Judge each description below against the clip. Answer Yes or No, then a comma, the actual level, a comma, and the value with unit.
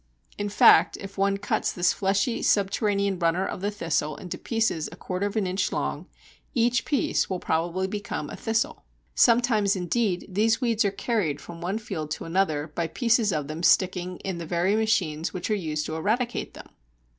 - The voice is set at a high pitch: Yes, high, 195 Hz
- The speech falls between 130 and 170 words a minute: No, average, 185 wpm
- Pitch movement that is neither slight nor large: Yes, average, 3.9 semitones